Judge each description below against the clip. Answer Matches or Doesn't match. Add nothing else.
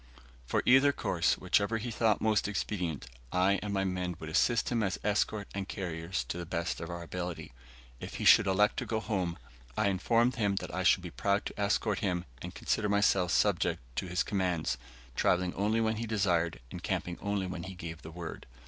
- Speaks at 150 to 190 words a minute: Doesn't match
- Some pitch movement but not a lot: Matches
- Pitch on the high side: Doesn't match